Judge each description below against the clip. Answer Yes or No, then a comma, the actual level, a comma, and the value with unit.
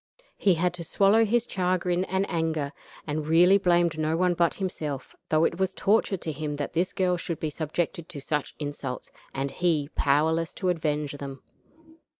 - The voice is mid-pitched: Yes, medium, 165 Hz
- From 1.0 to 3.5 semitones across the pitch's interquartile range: Yes, average, 3.2 semitones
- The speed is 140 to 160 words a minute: No, average, 175 wpm